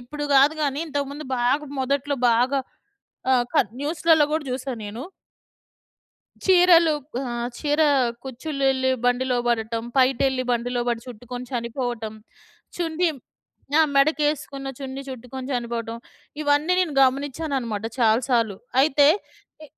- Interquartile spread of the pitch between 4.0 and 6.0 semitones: No, average, 3.4 semitones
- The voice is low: No, very high, 265 Hz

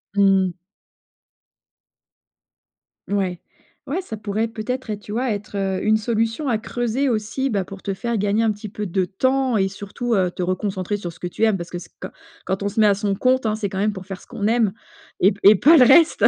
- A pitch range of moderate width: Yes, average, 3.0 semitones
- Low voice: No, high, 210 Hz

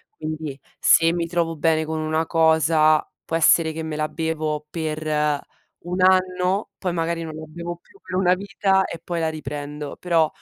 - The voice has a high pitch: No, medium, 160 Hz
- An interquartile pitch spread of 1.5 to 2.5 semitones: Yes, narrow, 1.8 semitones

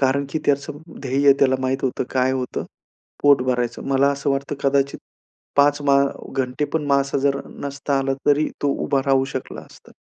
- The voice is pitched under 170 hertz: Yes, medium, 140 Hz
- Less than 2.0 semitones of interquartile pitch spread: Yes, narrow, 1.2 semitones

